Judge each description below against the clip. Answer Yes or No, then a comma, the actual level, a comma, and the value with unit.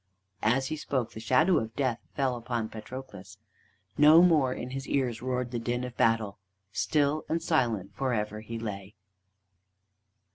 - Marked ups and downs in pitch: No, average, 3.5 semitones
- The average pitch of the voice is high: No, low, 125 Hz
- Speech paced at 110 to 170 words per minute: Yes, average, 155 wpm